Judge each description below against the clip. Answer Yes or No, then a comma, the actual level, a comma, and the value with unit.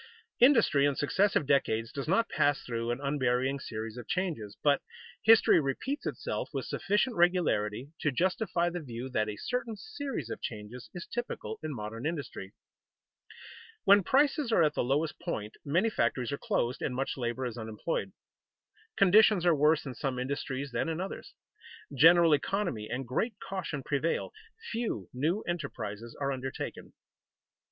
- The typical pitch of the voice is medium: Yes, medium, 145 Hz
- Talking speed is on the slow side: No, average, 155 wpm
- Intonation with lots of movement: Yes, wide, 6.7 semitones